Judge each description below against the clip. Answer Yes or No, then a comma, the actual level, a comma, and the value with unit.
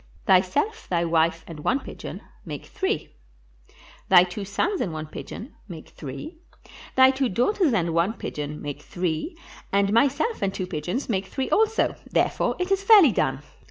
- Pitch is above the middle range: Yes, high, 195 Hz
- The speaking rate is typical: Yes, average, 165 wpm